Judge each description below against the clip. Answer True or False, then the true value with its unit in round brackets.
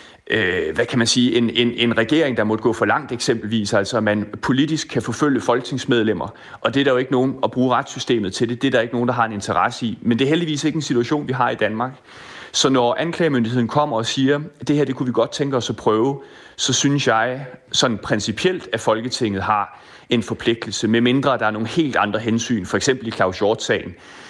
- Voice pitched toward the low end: True (120 Hz)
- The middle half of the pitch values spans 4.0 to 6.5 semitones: False (3.3 semitones)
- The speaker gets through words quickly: True (230 wpm)